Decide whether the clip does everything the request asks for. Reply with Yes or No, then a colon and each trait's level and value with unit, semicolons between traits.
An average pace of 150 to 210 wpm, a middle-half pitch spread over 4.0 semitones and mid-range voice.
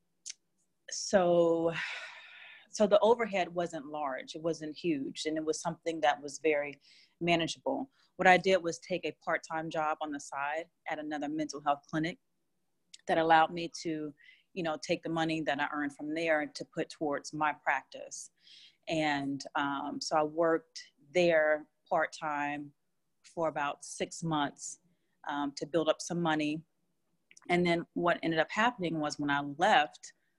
No: average, 155 wpm; narrow, 2.4 semitones; medium, 160 Hz